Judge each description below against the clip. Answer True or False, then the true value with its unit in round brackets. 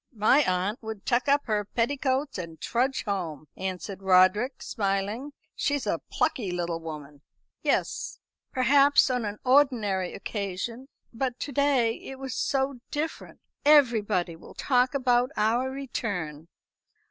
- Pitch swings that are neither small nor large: False (5.8 semitones)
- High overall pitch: True (230 Hz)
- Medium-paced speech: False (130 wpm)